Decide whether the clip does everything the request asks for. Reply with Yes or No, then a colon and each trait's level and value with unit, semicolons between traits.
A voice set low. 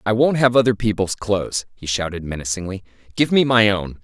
Yes: low, 105 Hz